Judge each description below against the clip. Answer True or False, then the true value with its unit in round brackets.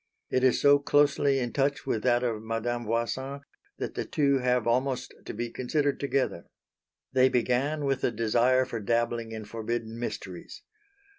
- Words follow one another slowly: False (160 wpm)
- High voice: False (125 Hz)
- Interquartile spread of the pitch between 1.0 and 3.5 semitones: True (2.7 semitones)